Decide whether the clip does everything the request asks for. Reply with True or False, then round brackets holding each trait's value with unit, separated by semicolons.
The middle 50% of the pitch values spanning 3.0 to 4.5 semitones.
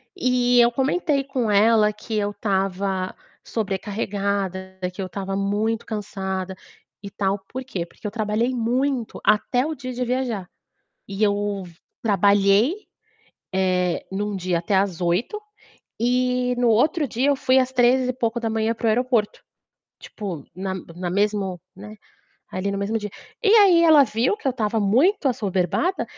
True (4.2 semitones)